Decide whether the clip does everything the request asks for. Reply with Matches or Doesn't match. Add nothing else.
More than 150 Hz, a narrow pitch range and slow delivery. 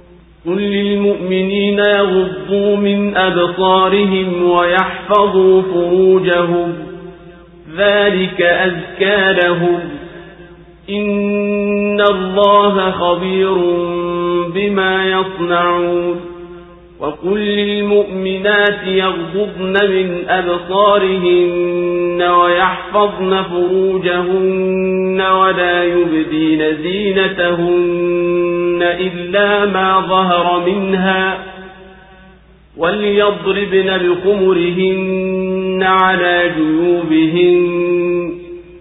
Matches